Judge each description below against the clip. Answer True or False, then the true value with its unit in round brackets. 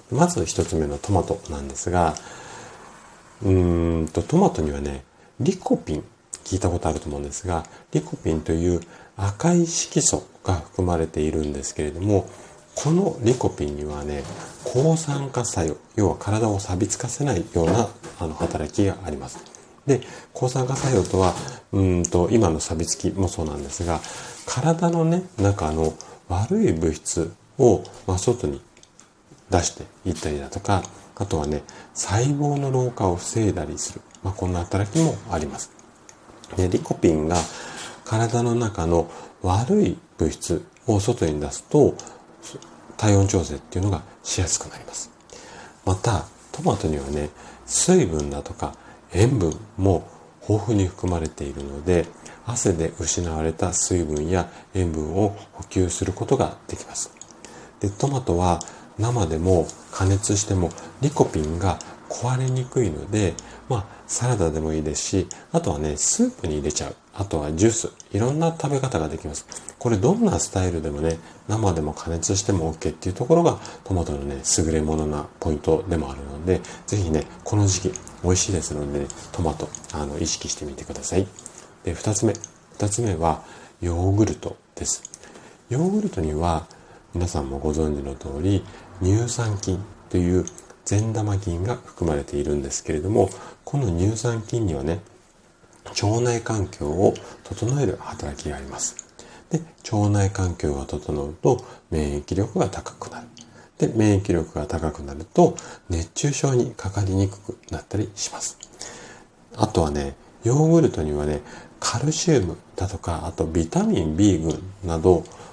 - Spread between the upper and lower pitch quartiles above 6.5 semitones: False (5.3 semitones)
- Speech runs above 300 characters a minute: False (295 characters per minute)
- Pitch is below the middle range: True (90 Hz)